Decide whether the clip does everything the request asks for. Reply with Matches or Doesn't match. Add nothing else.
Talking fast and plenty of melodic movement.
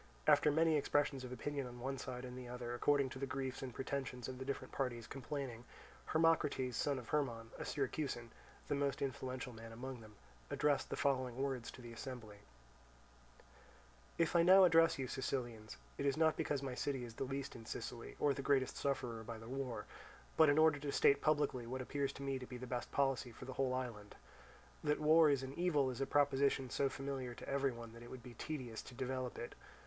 Doesn't match